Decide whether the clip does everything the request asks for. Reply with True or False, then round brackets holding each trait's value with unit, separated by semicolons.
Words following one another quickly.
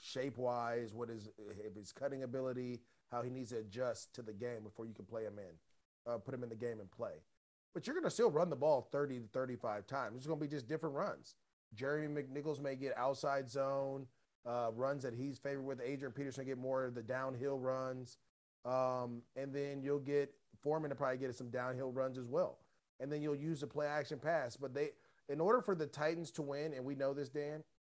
True (215 wpm)